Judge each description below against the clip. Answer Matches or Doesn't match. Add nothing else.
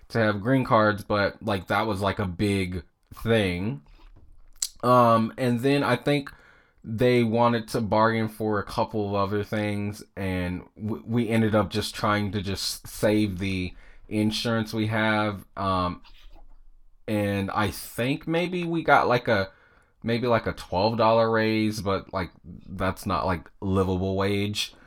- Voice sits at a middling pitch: Doesn't match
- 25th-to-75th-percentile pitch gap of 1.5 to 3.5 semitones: Matches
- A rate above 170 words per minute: Doesn't match